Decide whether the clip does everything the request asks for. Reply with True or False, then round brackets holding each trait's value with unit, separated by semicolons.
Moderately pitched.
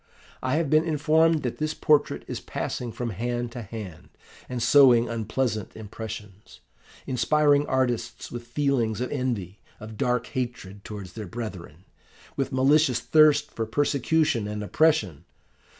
False (120 Hz)